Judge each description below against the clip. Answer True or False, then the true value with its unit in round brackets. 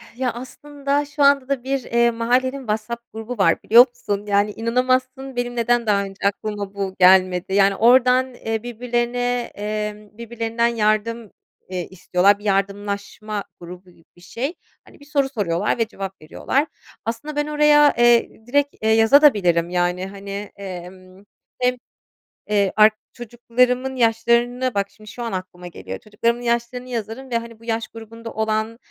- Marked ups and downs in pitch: False (3.6 semitones)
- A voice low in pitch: False (230 Hz)